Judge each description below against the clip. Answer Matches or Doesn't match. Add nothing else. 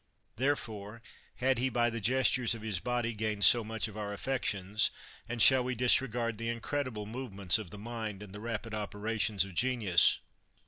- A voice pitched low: Matches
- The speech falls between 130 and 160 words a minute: Doesn't match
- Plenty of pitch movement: Doesn't match